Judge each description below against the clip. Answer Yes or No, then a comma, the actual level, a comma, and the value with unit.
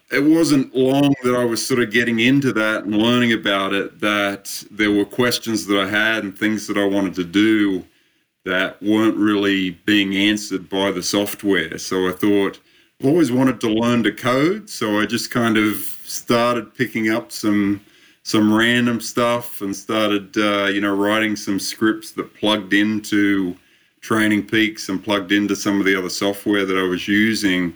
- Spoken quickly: No, average, 180 wpm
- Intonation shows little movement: Yes, narrow, 2.1 semitones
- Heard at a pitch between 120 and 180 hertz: No, low, 105 Hz